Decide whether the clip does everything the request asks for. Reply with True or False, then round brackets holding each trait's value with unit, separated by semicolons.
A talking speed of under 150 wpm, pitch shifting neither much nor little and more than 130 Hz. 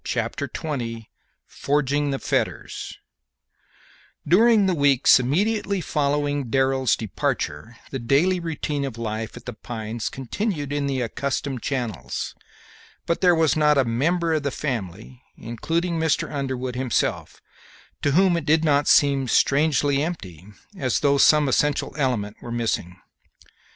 True (135 wpm; 4.2 semitones; 140 Hz)